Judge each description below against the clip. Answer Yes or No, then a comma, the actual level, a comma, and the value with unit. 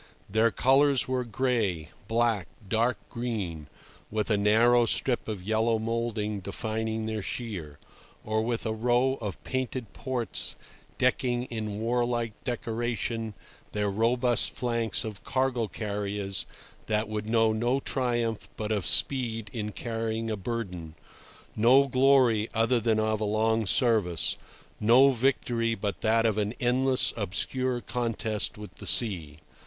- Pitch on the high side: No, low, 115 Hz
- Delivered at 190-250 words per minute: No, slow, 135 wpm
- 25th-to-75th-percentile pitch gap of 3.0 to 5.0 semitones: No, narrow, 2.4 semitones